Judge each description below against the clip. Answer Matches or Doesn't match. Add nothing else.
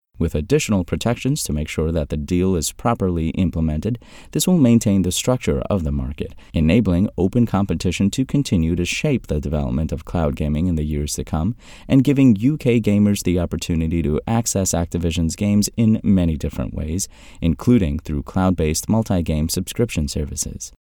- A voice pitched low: Matches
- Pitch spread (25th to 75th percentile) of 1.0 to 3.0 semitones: Doesn't match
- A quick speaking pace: Doesn't match